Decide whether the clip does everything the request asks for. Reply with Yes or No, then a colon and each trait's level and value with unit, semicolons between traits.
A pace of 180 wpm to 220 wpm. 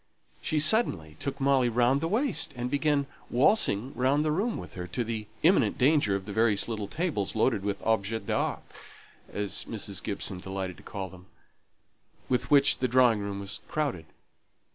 No: average, 170 wpm